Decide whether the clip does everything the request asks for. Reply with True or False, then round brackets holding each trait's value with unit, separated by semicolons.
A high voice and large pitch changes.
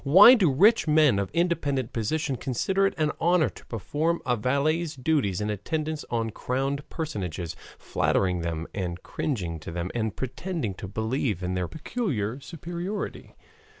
False (130 Hz; 7.9 semitones)